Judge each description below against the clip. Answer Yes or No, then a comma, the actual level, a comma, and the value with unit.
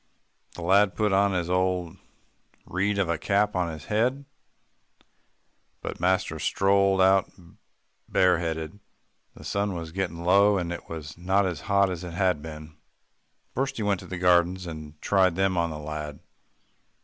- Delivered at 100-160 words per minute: Yes, average, 155 wpm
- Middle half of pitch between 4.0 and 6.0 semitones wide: No, average, 2.8 semitones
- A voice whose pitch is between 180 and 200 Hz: No, very low, 90 Hz